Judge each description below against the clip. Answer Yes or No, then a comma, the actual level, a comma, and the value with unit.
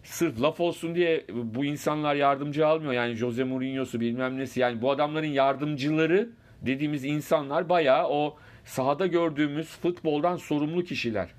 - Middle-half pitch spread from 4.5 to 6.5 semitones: No, average, 3.4 semitones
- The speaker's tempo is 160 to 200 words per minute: No, average, 135 wpm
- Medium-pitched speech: Yes, medium, 150 Hz